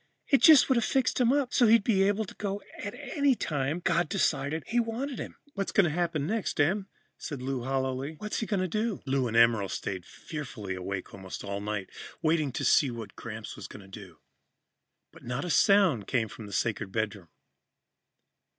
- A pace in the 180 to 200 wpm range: Yes, average, 195 wpm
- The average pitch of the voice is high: No, medium, 150 Hz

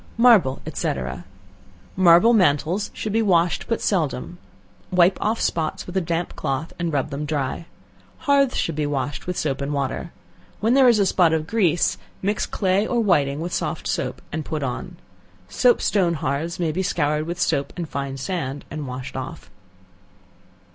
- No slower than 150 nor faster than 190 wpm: Yes, average, 170 wpm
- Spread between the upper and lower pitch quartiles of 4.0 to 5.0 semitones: Yes, average, 4.7 semitones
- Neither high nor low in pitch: Yes, medium, 170 Hz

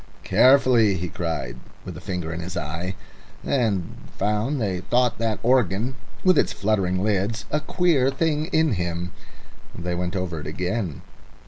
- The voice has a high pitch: No, low, 100 Hz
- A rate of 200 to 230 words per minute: No, average, 150 wpm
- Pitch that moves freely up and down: Yes, wide, 6.1 semitones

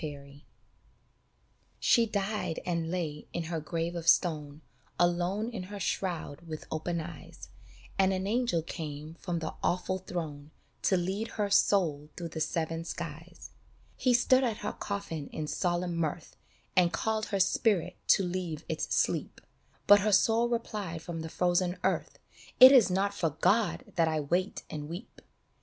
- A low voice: No, medium, 175 Hz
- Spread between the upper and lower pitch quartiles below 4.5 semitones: Yes, average, 3.6 semitones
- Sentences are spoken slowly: No, average, 160 wpm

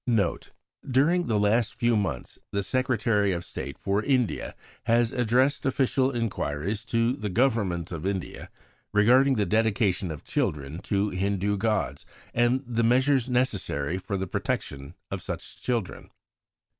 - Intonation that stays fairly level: No, average, 4.2 semitones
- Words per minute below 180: Yes, average, 140 wpm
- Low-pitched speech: Yes, low, 110 Hz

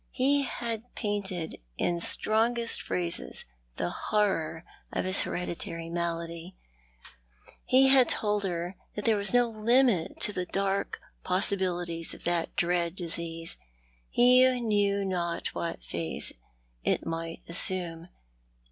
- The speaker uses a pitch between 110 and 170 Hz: No, medium, 185 Hz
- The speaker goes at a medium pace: No, slow, 120 wpm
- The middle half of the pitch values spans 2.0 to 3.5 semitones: No, average, 4.2 semitones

